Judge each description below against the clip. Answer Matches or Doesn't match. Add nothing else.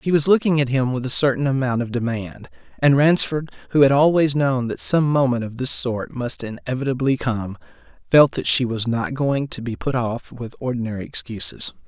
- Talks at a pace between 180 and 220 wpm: Matches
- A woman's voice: Doesn't match